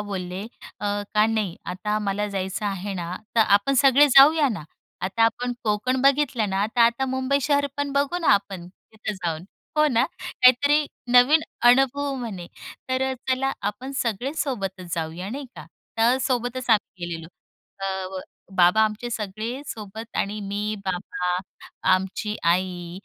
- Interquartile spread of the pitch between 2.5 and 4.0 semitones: No, average, 5.2 semitones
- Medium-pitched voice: No, high, 215 Hz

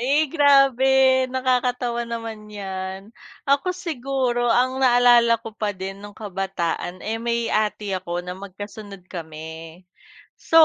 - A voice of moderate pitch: No, high, 230 Hz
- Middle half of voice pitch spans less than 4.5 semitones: No, average, 4.9 semitones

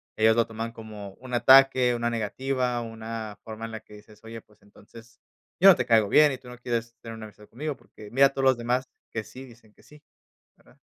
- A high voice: No, low, 115 Hz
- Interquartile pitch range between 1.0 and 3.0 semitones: Yes, narrow, 2.4 semitones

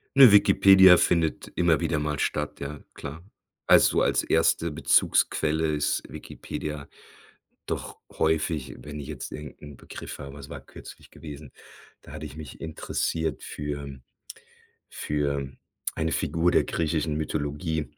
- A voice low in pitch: Yes, very low, 75 Hz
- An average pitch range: No, narrow, 1.9 semitones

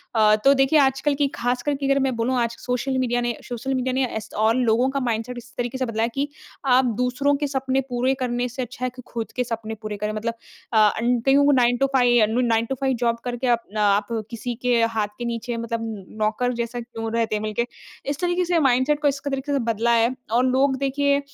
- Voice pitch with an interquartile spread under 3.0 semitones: Yes, narrow, 2.5 semitones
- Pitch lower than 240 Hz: No, high, 245 Hz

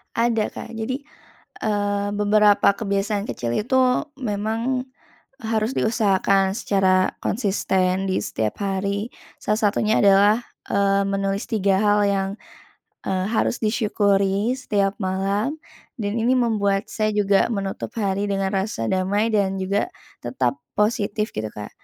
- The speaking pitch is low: No, high, 205 Hz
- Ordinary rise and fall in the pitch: No, narrow, 2.0 semitones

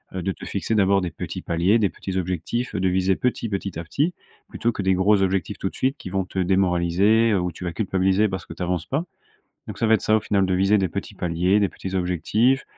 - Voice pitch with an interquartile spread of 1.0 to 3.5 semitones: Yes, average, 2.7 semitones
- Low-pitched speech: Yes, very low, 95 Hz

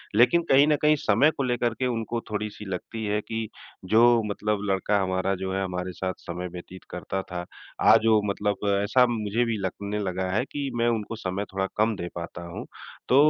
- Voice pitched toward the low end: Yes, low, 105 Hz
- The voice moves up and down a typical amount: Yes, average, 3.6 semitones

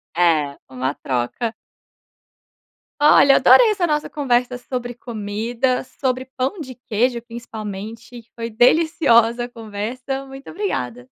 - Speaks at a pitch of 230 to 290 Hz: Yes, high, 240 Hz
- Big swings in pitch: No, average, 3.5 semitones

